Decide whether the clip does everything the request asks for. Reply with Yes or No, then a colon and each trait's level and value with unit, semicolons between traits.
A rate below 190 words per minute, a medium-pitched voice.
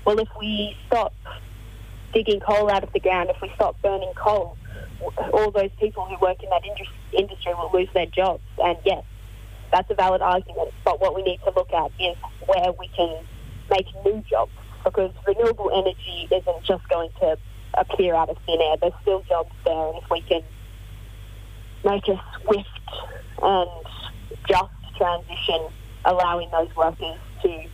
Yes: average, 165 wpm; medium, 180 Hz